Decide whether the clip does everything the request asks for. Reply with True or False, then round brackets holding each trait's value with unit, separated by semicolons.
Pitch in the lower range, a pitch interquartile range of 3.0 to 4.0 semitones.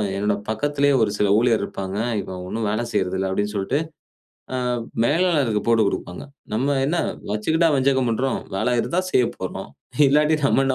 False (120 Hz; 5.4 semitones)